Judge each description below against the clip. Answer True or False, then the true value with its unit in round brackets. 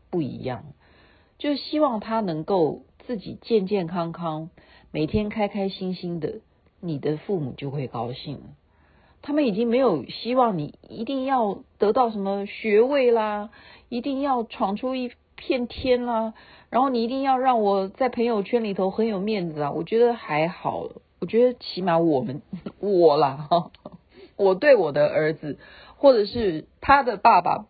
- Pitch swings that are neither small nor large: False (6.6 semitones)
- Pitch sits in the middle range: False (205 Hz)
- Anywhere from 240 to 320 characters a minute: False (225 characters per minute)